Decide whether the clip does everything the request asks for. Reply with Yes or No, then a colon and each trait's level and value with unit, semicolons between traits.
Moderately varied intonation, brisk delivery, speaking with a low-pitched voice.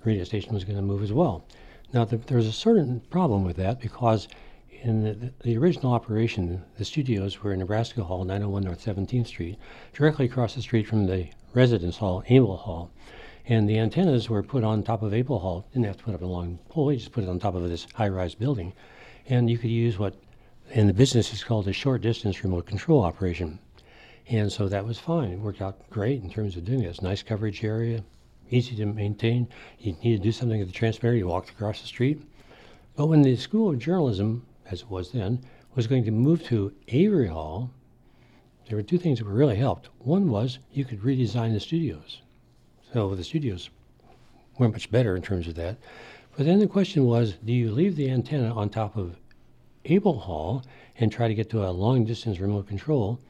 Yes: average, 3.8 semitones; fast, 210 wpm; low, 115 Hz